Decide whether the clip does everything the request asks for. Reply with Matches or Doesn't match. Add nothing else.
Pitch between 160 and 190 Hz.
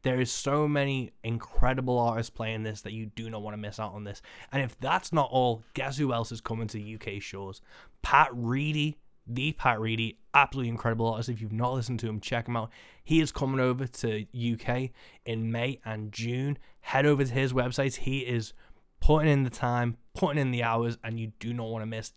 Doesn't match